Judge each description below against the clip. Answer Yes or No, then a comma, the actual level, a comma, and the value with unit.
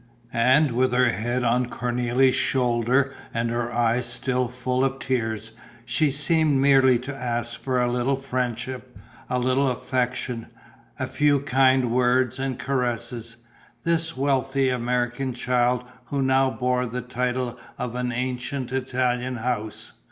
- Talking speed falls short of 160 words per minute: Yes, slow, 135 wpm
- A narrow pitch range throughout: Yes, narrow, 1.4 semitones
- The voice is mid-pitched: No, low, 125 Hz